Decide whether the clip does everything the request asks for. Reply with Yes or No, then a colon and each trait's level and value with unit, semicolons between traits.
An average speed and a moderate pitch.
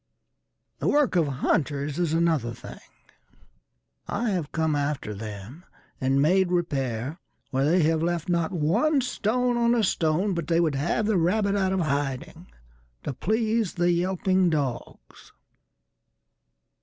No: slow, 125 wpm; medium, 165 Hz